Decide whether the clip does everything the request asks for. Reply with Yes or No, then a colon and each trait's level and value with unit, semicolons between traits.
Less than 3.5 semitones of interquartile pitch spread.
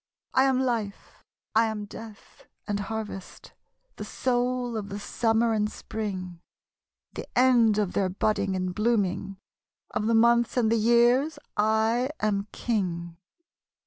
Yes: average, 2.8 semitones